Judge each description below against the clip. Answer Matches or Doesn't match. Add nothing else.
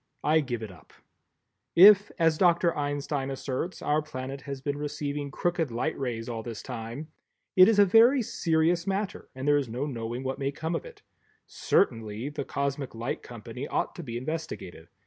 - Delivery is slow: Doesn't match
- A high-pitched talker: Doesn't match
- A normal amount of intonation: Matches